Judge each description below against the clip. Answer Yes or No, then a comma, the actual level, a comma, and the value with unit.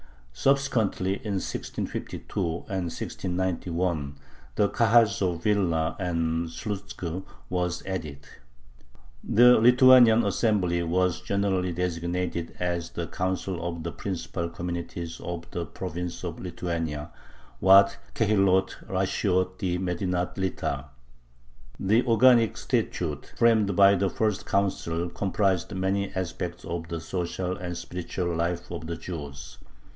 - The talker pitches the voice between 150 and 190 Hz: No, very low, 90 Hz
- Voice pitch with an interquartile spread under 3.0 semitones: Yes, narrow, 2.6 semitones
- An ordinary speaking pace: No, slow, 115 wpm